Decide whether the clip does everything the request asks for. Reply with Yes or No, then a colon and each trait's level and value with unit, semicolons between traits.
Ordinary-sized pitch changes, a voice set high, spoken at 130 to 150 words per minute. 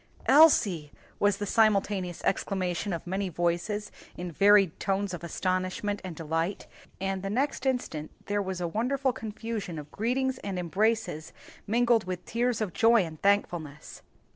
Yes: average, 4.0 semitones; high, 195 Hz; average, 145 wpm